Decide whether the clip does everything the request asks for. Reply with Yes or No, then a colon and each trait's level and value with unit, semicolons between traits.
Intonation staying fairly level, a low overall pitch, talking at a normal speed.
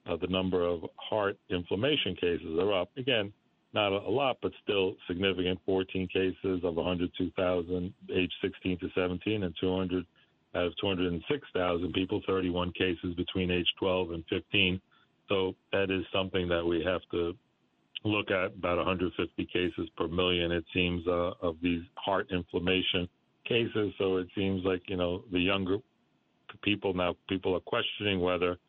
Yes: narrow, 1.3 semitones; very low, 90 Hz; average, 155 wpm